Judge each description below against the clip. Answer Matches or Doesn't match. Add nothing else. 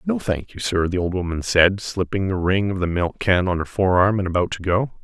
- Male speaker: Matches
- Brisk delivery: Matches